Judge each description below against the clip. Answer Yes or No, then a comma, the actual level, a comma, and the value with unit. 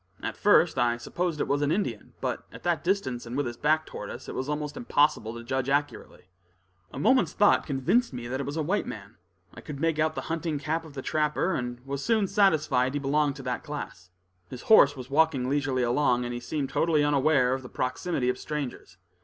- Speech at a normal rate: No, fast, 220 wpm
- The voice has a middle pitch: Yes, medium, 145 Hz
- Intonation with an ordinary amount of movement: Yes, average, 3.7 semitones